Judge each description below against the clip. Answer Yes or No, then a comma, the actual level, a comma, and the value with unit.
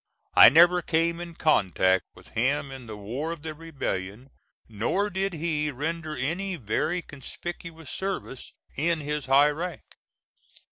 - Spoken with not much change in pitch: No, average, 4.2 semitones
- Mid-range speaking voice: Yes, medium, 155 Hz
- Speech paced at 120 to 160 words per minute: Yes, average, 140 wpm